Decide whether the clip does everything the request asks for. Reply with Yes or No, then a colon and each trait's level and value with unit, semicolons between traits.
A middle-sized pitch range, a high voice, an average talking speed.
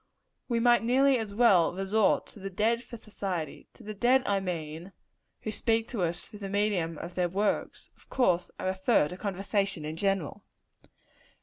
Yes: average, 3.8 semitones; high, 200 Hz; average, 180 wpm